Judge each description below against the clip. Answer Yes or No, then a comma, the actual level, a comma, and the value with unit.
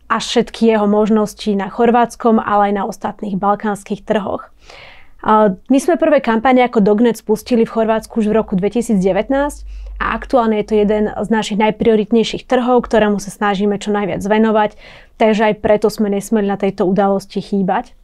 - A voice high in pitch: Yes, high, 215 Hz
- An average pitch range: No, narrow, 1.7 semitones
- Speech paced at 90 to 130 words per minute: No, fast, 165 wpm